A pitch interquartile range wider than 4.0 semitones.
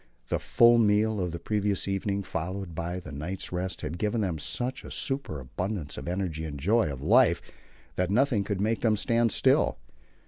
Yes: average, 4.4 semitones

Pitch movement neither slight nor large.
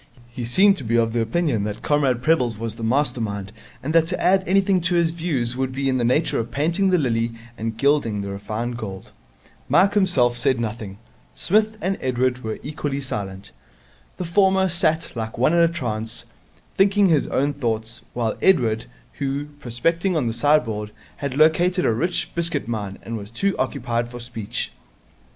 No: wide, 6.5 semitones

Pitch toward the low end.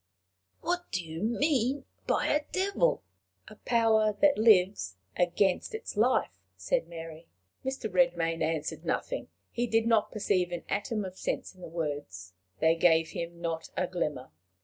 No: medium, 185 Hz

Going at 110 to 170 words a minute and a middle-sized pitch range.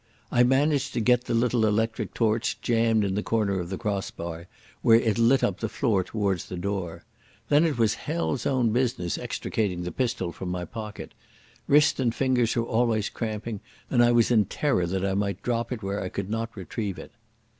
No: average, 200 wpm; average, 3.5 semitones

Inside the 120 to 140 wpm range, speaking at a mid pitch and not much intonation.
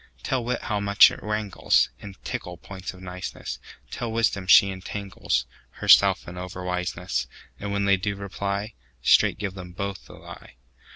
No: slow, 135 wpm; low, 100 Hz; narrow, 2.0 semitones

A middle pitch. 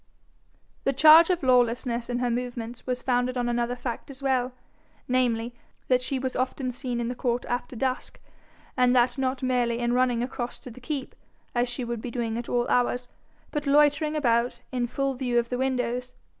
No: very high, 250 Hz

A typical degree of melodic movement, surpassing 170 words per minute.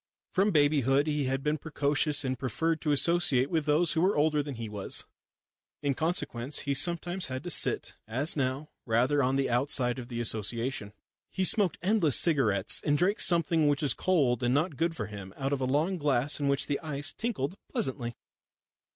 Yes: average, 3.8 semitones; average, 190 wpm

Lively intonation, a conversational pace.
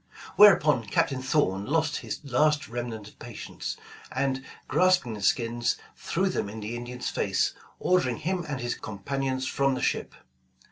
No: average, 4.1 semitones; average, 155 wpm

